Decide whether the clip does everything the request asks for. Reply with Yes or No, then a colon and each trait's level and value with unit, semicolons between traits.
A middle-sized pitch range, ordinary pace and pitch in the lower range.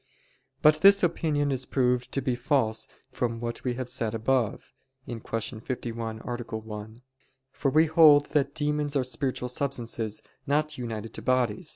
Yes: average, 4.1 semitones; average, 155 wpm; low, 125 Hz